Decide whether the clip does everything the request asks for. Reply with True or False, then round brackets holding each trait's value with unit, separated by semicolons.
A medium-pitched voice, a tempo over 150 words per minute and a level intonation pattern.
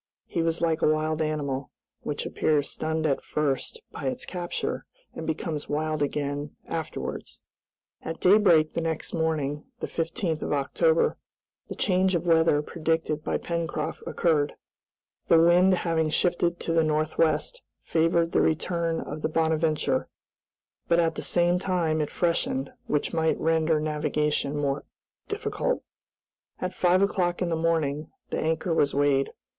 False (160 Hz; 145 wpm; 2.1 semitones)